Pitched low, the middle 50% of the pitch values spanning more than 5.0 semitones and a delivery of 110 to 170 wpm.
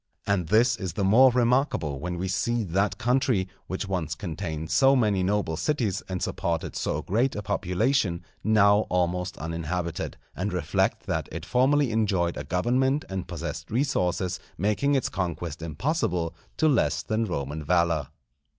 Yes: very low, 95 Hz; wide, 5.6 semitones; average, 150 wpm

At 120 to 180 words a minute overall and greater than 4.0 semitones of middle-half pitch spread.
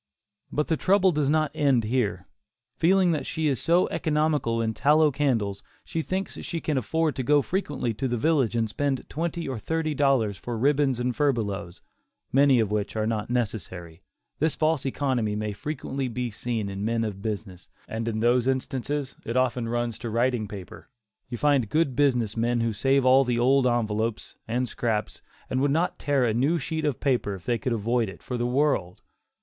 No: average, 190 wpm; average, 4.5 semitones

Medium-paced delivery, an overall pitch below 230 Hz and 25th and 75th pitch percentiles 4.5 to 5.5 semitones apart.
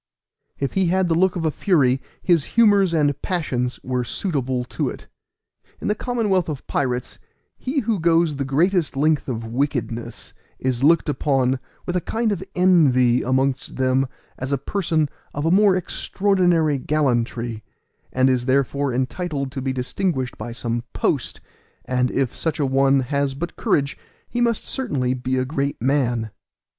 Yes: average, 160 wpm; medium, 140 Hz; average, 5.2 semitones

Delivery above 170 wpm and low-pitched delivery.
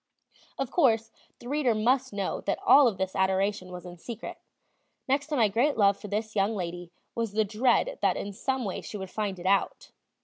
No: fast, 205 wpm; high, 215 Hz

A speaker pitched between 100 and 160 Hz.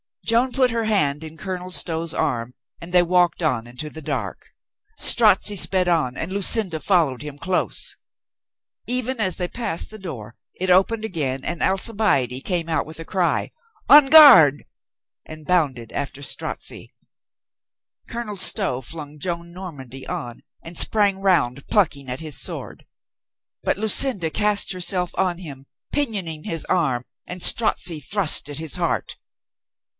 No: medium, 175 Hz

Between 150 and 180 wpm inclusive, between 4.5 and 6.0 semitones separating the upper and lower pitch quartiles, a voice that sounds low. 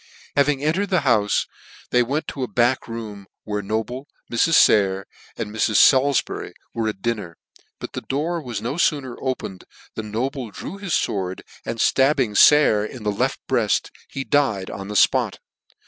Yes: average, 170 wpm; average, 5.1 semitones; low, 120 Hz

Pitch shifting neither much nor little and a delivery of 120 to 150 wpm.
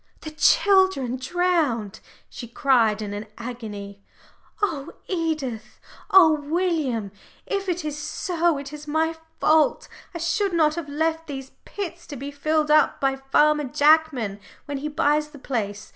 Yes: average, 4.0 semitones; average, 145 wpm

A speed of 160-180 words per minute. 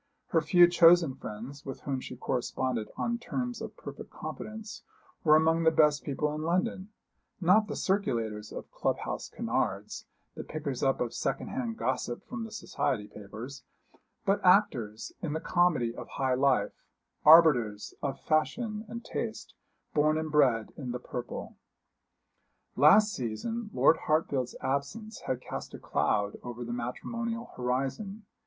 No: average, 150 wpm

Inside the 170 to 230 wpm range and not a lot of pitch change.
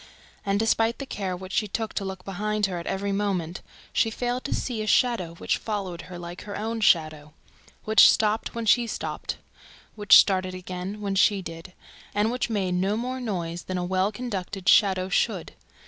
No: average, 190 wpm; average, 3.0 semitones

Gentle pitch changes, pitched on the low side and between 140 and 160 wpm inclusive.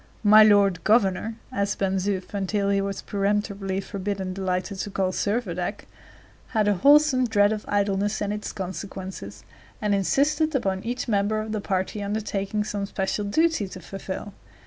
No: narrow, 1.8 semitones; high, 200 Hz; average, 155 wpm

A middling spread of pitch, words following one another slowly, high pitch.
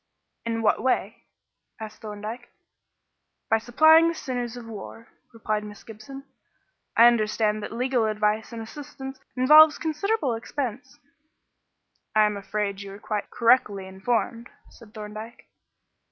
Yes: average, 3.3 semitones; slow, 125 wpm; high, 225 Hz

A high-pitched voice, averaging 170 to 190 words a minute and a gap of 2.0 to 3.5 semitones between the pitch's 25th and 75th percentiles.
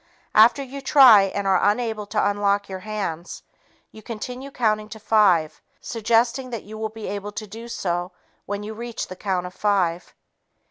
Yes: high, 210 Hz; average, 175 wpm; narrow, 2.5 semitones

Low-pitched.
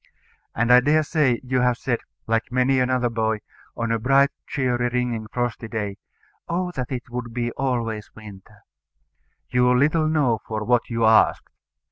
Yes: low, 120 Hz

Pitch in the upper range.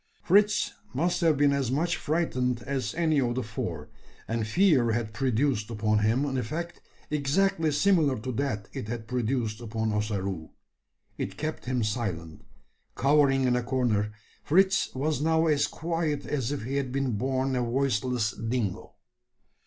No: low, 130 Hz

